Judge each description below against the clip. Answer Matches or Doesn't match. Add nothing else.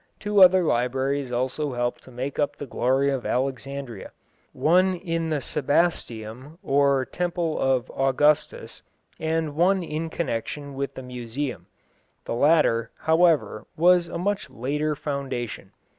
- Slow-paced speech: Matches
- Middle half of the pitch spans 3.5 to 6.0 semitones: Matches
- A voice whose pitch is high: Doesn't match